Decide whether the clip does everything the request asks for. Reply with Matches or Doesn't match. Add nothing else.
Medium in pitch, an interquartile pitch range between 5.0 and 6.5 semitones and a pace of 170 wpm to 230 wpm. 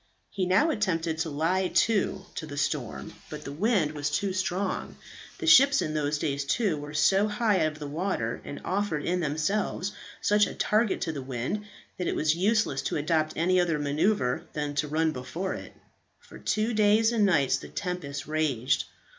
Matches